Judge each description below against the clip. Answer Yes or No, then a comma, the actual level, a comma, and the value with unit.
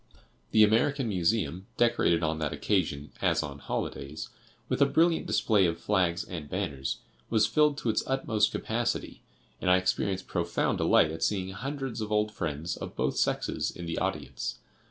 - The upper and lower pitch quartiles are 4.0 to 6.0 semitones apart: Yes, average, 5.3 semitones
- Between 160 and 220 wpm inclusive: Yes, average, 165 wpm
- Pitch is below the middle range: Yes, very low, 95 Hz